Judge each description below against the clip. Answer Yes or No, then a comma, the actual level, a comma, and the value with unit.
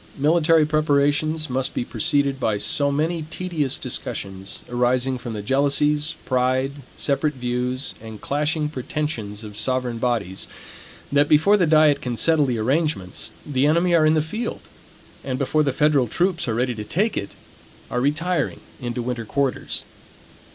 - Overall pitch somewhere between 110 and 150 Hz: Yes, medium, 140 Hz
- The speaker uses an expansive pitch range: No, average, 3.9 semitones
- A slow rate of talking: No, average, 150 wpm